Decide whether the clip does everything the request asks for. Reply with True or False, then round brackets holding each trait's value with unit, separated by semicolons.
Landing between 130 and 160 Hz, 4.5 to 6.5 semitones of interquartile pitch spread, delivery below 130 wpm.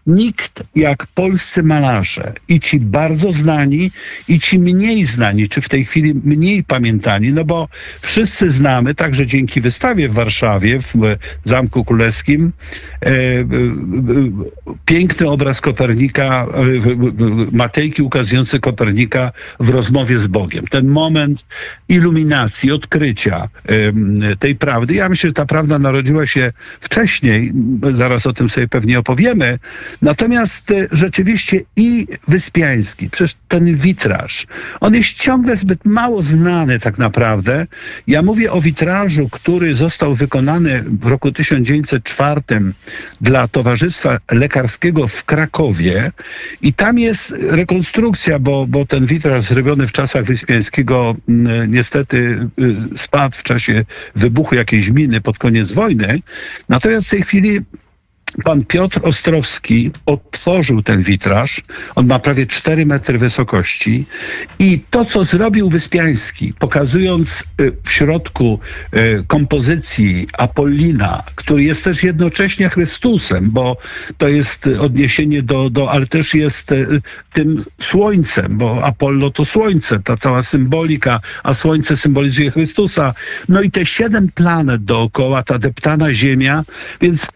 True (140 Hz; 5.2 semitones; 120 wpm)